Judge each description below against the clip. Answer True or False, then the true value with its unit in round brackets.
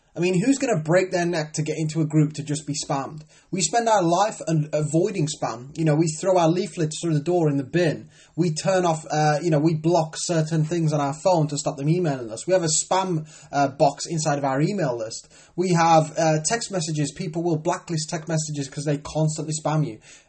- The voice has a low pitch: False (160 Hz)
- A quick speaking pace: True (235 wpm)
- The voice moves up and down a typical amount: False (2.3 semitones)